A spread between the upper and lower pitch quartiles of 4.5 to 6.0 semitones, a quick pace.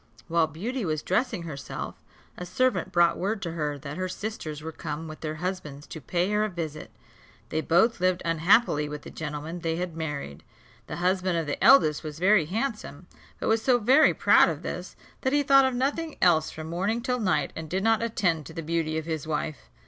Yes: wide, 5.4 semitones; fast, 210 wpm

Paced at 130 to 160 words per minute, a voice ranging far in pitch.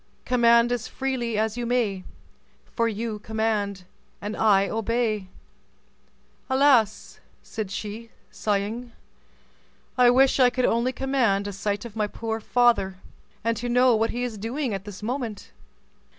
No: average, 140 wpm; average, 2.7 semitones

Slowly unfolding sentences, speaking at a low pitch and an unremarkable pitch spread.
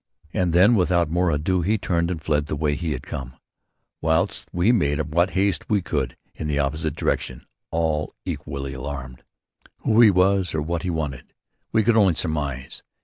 No: average, 180 wpm; very low, 80 Hz; average, 4.0 semitones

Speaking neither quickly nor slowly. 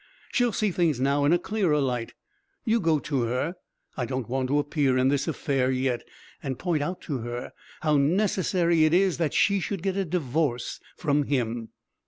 Yes: average, 190 wpm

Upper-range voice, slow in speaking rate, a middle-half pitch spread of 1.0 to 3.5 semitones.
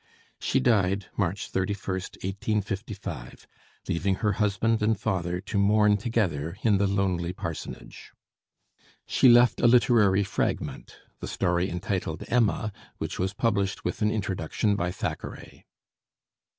No: low, 100 Hz; slow, 125 wpm; narrow, 2.6 semitones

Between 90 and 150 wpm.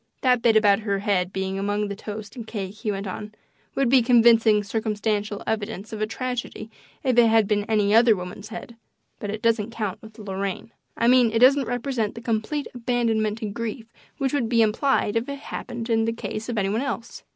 No: fast, 205 wpm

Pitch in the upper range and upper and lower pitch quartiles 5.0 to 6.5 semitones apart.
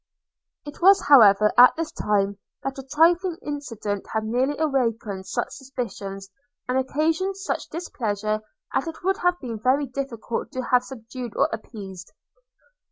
Yes: very high, 255 Hz; wide, 5.6 semitones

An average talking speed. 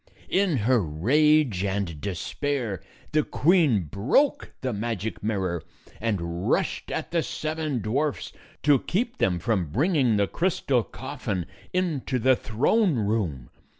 No: slow, 125 wpm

